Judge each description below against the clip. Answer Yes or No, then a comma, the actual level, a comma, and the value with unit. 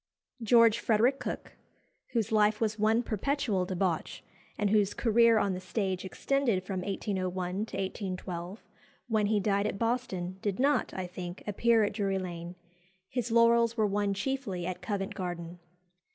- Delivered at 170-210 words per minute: No, average, 150 wpm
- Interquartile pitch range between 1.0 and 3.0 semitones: No, average, 3.6 semitones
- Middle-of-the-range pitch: No, high, 205 Hz